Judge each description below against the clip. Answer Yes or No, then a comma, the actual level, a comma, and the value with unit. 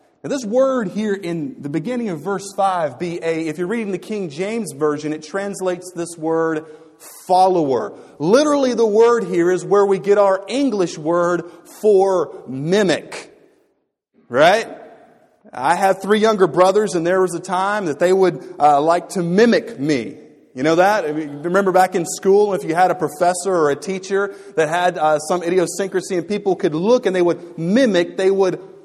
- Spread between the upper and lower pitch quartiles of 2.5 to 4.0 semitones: Yes, average, 3.1 semitones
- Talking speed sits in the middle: Yes, average, 175 wpm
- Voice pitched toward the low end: No, medium, 185 Hz